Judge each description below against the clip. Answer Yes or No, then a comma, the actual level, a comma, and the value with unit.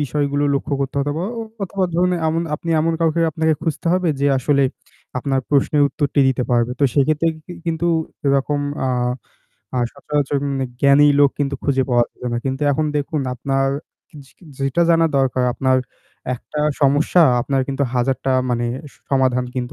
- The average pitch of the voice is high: No, medium, 140 Hz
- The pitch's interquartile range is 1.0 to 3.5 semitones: Yes, narrow, 2.6 semitones